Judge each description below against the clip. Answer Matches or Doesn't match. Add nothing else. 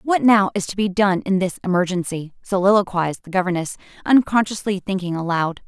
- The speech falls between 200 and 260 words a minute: Doesn't match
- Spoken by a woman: Matches